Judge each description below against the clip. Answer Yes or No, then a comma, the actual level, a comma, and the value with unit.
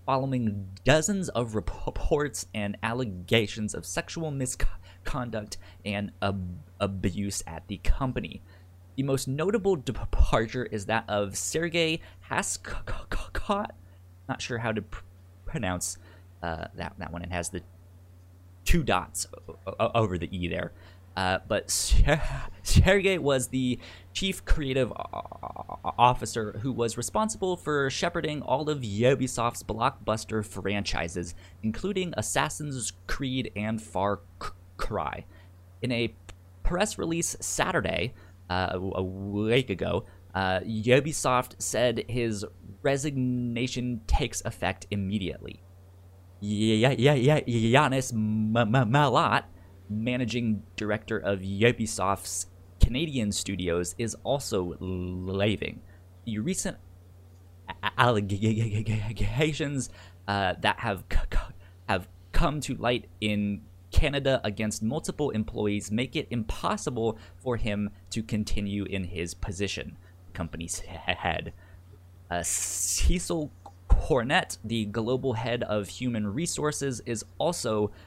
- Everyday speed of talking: No, slow, 110 wpm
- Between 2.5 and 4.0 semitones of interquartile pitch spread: No, average, 5.1 semitones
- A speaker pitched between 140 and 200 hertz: No, low, 105 Hz